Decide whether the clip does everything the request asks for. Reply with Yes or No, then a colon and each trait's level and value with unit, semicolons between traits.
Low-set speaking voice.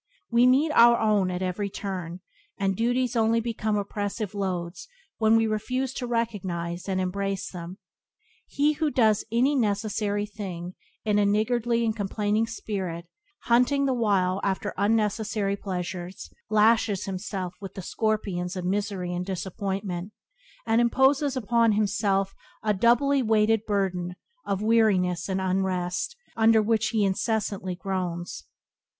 No: high, 205 Hz